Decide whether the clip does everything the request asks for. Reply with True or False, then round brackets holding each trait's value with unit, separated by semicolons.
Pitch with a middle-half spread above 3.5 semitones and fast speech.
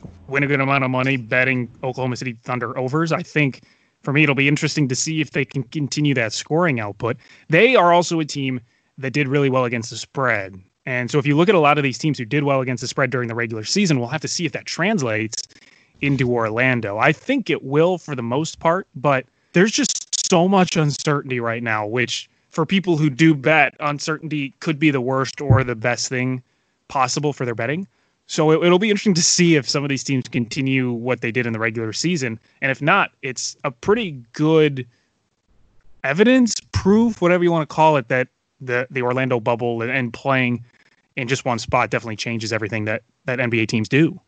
True (4.2 semitones; 215 wpm)